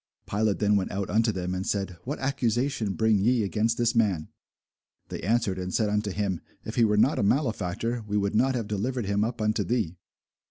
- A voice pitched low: Yes, low, 105 Hz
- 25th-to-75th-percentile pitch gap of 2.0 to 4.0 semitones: Yes, average, 2.9 semitones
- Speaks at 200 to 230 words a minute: Yes, fast, 205 wpm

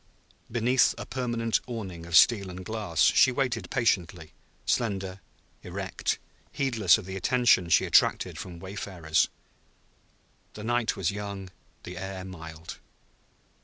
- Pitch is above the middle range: No, very low, 95 Hz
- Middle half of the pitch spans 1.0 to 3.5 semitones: No, average, 4.3 semitones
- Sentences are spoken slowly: Yes, slow, 125 wpm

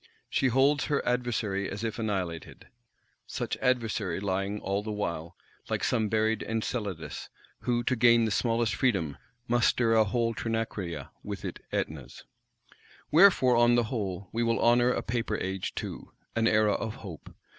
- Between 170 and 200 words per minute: No, average, 155 wpm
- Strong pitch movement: No, average, 3.3 semitones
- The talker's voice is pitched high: No, low, 110 Hz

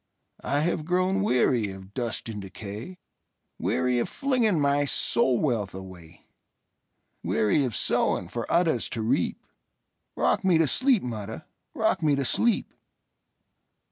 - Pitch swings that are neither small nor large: No, wide, 7.9 semitones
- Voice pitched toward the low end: Yes, low, 125 Hz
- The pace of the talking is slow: Yes, slow, 115 wpm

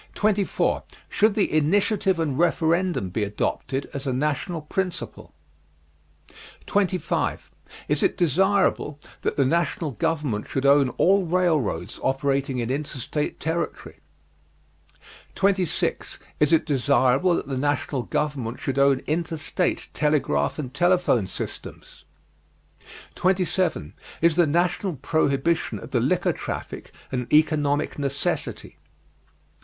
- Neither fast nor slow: No, slow, 110 wpm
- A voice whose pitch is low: No, medium, 150 Hz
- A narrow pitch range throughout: No, average, 4.3 semitones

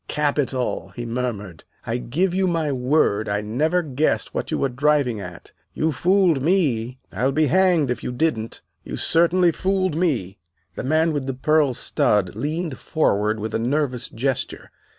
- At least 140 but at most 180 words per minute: Yes, average, 165 wpm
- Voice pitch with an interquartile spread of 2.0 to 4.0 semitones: No, average, 5.3 semitones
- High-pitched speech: No, medium, 140 Hz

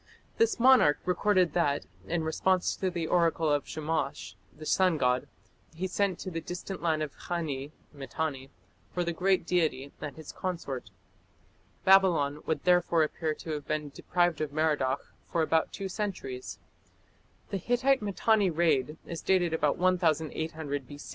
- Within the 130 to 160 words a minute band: Yes, average, 150 wpm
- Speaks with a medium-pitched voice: Yes, medium, 165 Hz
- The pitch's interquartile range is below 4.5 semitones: Yes, average, 3.6 semitones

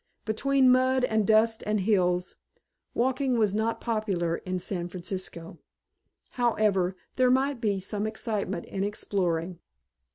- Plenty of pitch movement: No, average, 4.1 semitones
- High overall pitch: Yes, high, 210 Hz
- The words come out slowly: Yes, slow, 125 wpm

